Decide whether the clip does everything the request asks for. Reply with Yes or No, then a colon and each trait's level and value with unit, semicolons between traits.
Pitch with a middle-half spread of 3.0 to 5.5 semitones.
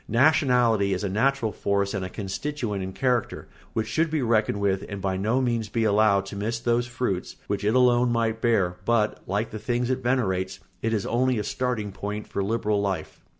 Yes: average, 3.3 semitones